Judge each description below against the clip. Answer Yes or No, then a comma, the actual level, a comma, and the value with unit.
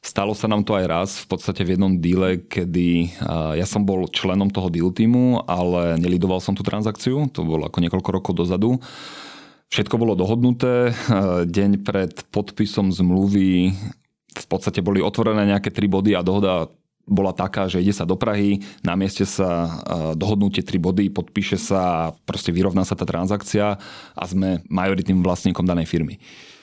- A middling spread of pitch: No, narrow, 2.2 semitones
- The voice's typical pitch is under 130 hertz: Yes, very low, 95 Hz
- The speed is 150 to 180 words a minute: Yes, fast, 165 wpm